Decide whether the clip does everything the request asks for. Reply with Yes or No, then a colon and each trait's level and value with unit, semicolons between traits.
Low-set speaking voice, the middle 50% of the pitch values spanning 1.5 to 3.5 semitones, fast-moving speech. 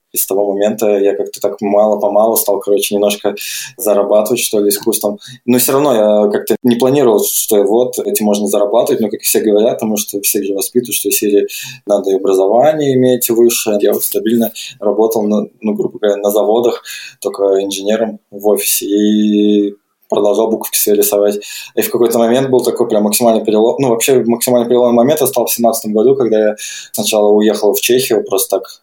Yes: low, 105 Hz; average, 2.8 semitones; fast, 185 wpm